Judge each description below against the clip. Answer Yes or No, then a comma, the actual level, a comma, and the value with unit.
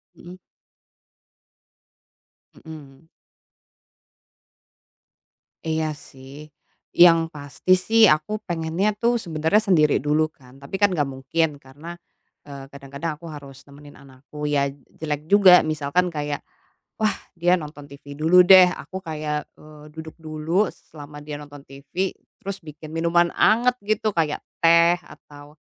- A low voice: No, medium, 155 Hz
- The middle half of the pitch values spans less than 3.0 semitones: No, average, 3.4 semitones